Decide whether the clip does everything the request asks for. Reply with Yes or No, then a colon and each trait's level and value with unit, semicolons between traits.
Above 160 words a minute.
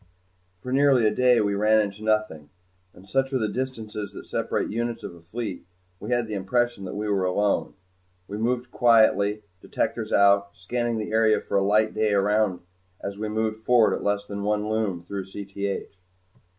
Yes: average, 185 wpm